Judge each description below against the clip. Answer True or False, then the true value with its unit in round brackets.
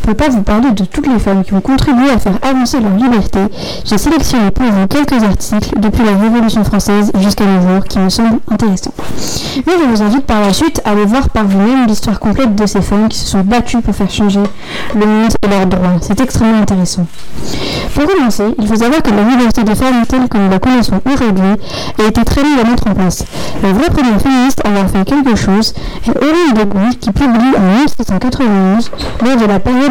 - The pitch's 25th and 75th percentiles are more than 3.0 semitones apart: True (4.0 semitones)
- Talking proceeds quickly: True (225 wpm)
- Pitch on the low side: False (215 Hz)